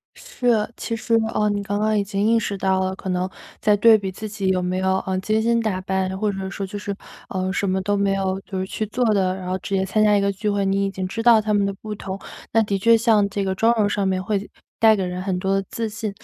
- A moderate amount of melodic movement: No, narrow, 2.2 semitones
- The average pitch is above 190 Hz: Yes, high, 200 Hz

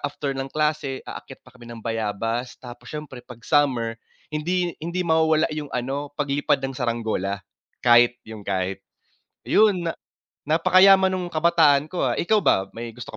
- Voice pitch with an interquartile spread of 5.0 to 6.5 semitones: Yes, average, 5.3 semitones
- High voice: No, medium, 140 Hz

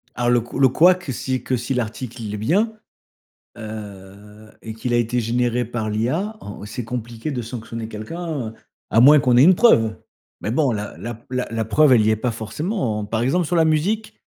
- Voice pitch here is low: Yes, low, 120 Hz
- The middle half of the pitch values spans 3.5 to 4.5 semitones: Yes, average, 4.0 semitones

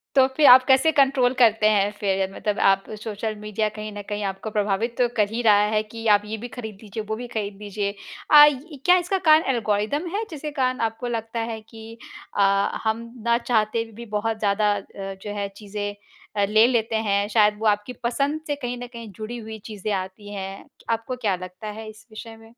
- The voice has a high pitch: Yes, high, 220 Hz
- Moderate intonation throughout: No, narrow, 2.3 semitones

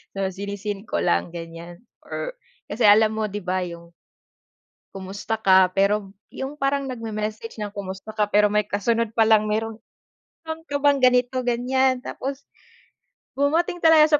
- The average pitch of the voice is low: No, high, 215 Hz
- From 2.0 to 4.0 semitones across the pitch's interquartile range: No, average, 4.7 semitones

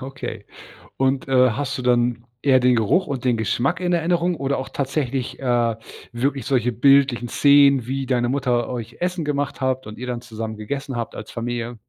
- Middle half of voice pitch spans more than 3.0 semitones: No, average, 2.7 semitones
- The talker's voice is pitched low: Yes, low, 130 Hz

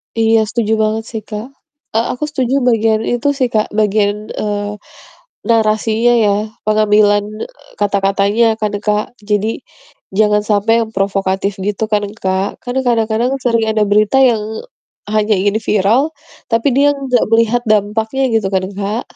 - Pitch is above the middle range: Yes, high, 220 Hz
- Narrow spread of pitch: Yes, narrow, 2.0 semitones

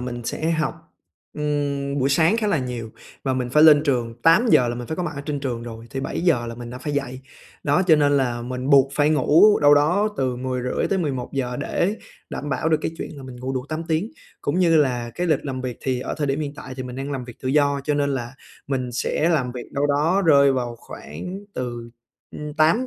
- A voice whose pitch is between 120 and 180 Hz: Yes, medium, 140 Hz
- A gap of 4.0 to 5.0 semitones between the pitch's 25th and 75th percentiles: No, average, 3.5 semitones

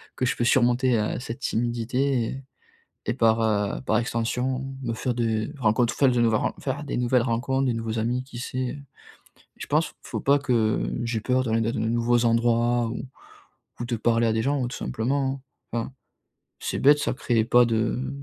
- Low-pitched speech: Yes, low, 120 Hz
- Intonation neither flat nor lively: No, narrow, 2.2 semitones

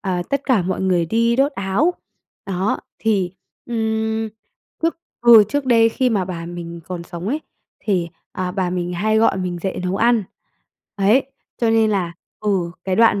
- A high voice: Yes, high, 200 Hz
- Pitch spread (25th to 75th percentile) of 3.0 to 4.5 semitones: Yes, average, 3.9 semitones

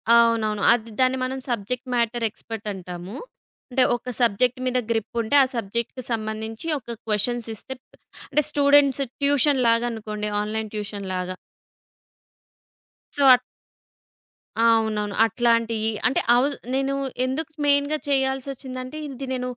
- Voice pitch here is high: Yes, high, 235 Hz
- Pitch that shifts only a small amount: No, average, 3.3 semitones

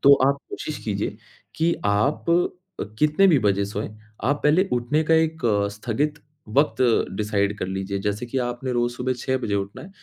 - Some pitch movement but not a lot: No, wide, 6.7 semitones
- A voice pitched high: No, low, 125 Hz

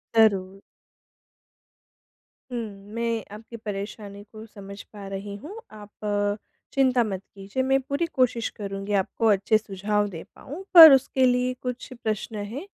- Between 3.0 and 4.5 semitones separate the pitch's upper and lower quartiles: Yes, average, 4.0 semitones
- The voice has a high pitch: Yes, high, 220 Hz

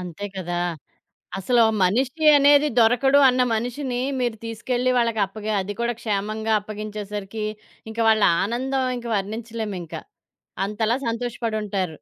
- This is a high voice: Yes, high, 220 Hz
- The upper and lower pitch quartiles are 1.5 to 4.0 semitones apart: Yes, average, 3.0 semitones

